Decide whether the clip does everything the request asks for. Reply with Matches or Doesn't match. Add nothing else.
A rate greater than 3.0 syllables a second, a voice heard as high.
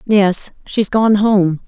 Doesn't match